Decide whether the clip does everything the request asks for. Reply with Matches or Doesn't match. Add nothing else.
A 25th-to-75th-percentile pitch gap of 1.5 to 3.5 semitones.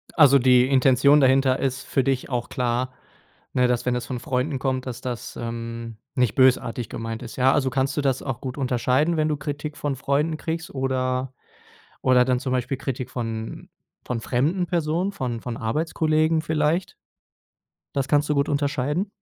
Matches